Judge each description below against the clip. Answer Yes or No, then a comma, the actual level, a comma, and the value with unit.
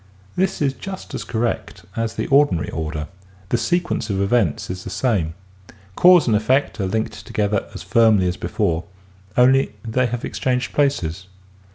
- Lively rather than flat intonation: Yes, wide, 6.0 semitones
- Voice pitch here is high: No, low, 110 Hz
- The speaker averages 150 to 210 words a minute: Yes, average, 165 wpm